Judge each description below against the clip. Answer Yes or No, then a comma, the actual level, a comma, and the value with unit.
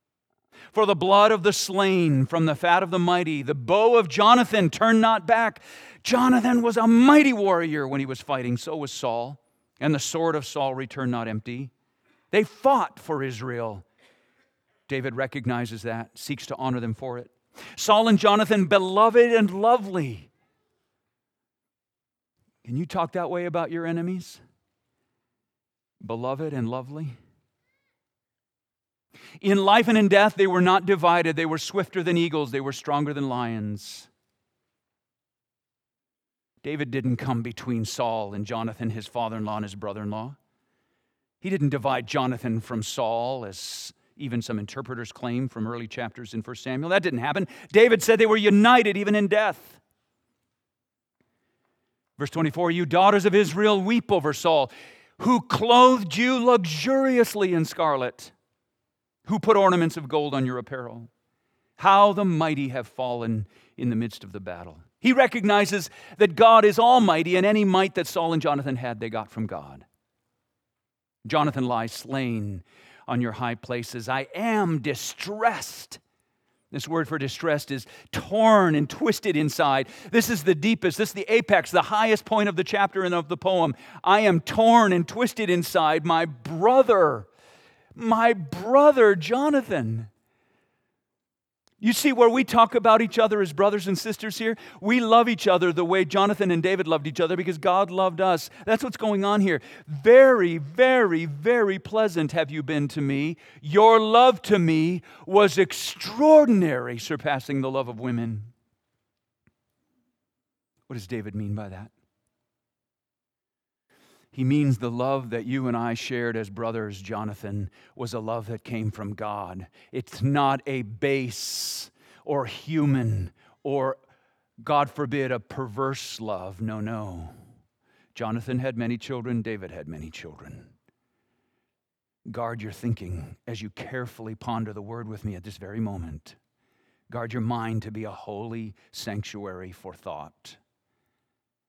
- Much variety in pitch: Yes, wide, 9.0 semitones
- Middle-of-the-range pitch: Yes, medium, 145 Hz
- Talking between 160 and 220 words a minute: No, average, 150 wpm